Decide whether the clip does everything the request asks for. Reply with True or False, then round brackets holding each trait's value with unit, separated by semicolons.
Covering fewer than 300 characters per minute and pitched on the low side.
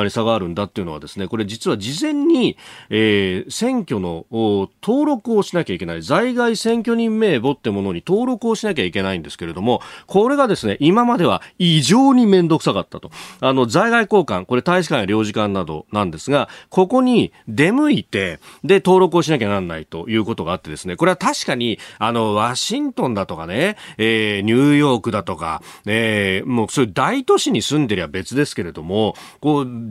False (395 characters per minute; 130 Hz)